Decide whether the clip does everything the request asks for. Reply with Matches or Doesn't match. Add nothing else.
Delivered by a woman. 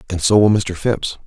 Doesn't match